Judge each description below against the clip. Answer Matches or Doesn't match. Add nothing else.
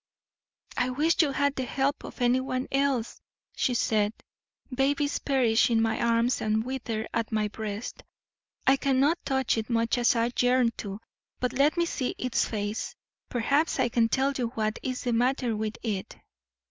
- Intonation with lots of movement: Doesn't match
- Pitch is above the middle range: Matches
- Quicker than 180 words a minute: Doesn't match